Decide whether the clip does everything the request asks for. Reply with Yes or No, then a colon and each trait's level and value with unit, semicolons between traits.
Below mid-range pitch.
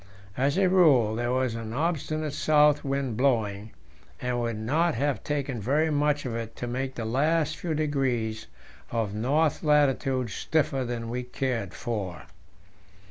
Yes: low, 130 Hz